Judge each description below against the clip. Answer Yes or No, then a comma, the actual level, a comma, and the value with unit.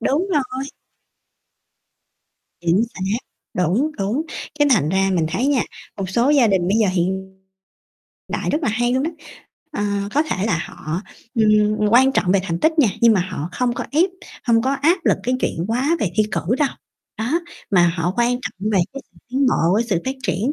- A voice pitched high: Yes, high, 225 Hz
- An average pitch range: No, wide, 5.9 semitones